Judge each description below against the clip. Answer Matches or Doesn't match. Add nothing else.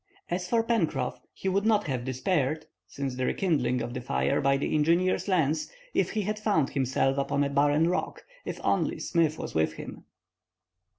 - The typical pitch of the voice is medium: Matches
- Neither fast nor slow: Matches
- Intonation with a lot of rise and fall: Matches